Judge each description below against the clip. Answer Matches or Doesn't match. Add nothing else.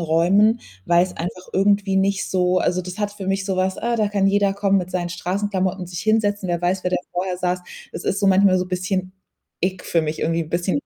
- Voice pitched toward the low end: Doesn't match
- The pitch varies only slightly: Matches